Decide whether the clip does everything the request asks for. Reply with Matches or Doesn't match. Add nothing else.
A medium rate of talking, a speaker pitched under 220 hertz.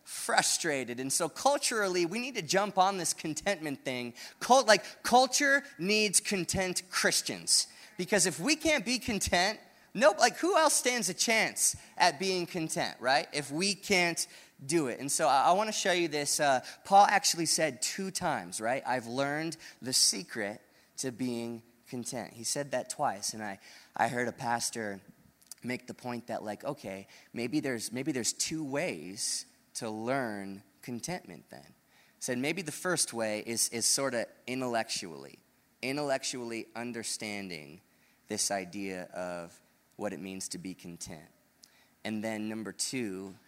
Matches